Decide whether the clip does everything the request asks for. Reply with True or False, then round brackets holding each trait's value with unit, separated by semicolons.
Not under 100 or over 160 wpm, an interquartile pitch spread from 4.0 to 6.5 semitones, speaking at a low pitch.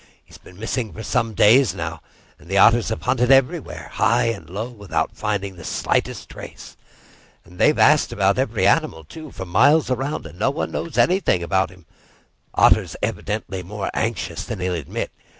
False (170 wpm; 5.4 semitones; 105 Hz)